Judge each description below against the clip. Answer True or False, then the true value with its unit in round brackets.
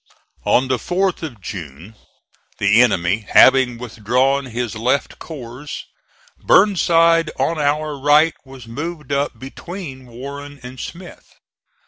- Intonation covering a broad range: False (4.4 semitones)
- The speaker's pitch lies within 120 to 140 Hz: True (135 Hz)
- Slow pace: True (115 wpm)